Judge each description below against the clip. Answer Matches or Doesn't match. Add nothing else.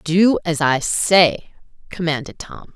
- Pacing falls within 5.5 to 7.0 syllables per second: Doesn't match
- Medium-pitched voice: Matches